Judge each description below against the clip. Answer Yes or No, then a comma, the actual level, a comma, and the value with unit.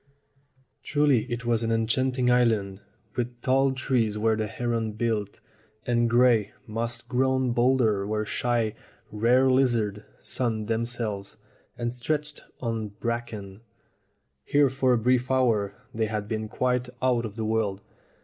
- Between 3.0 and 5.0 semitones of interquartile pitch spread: No, narrow, 2.5 semitones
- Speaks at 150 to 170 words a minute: No, slow, 135 wpm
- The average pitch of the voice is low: Yes, low, 115 Hz